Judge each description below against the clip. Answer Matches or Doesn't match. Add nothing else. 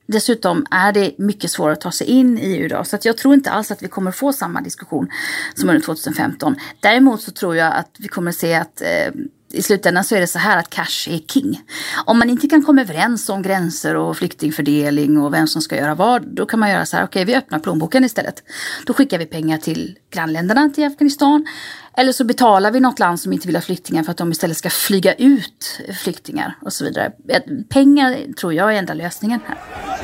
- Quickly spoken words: Matches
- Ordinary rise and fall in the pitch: Doesn't match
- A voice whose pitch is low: Doesn't match